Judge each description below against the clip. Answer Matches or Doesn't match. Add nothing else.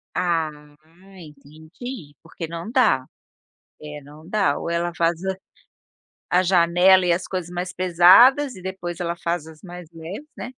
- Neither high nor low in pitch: Matches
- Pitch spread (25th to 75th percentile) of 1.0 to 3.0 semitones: Matches